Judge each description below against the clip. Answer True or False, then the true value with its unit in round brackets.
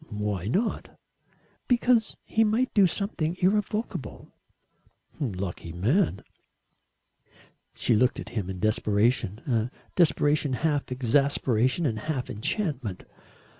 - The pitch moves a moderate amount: False (9.0 semitones)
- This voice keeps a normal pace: False (100 wpm)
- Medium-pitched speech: False (130 Hz)